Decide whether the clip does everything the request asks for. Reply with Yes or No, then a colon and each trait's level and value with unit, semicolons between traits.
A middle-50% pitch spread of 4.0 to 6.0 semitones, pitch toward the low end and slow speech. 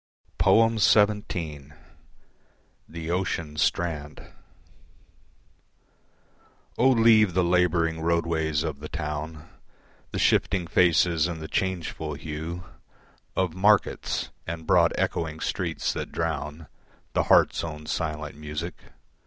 No: average, 2.7 semitones; very low, 80 Hz; slow, 100 wpm